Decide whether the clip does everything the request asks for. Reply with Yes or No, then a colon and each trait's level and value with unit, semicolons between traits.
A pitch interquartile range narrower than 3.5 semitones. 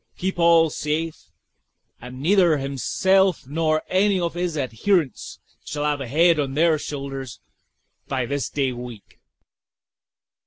No: average, 4.0 semitones